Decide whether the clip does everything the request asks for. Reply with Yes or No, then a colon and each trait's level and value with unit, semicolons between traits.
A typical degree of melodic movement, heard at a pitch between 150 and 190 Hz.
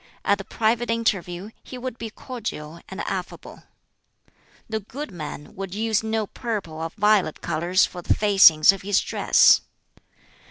No: average, 3.9 semitones; high, 200 Hz